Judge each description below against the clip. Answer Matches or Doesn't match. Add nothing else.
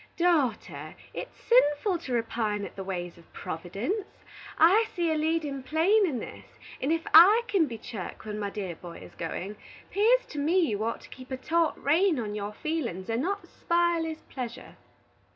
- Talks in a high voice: Matches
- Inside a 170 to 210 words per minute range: Matches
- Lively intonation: Matches